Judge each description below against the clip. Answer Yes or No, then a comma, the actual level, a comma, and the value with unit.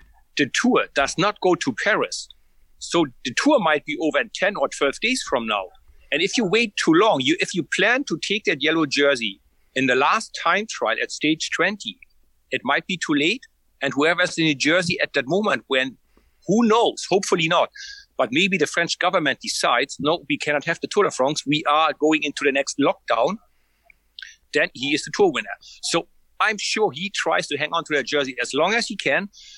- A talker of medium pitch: Yes, medium, 170 Hz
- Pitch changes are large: Yes, wide, 7.4 semitones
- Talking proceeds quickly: Yes, fast, 210 wpm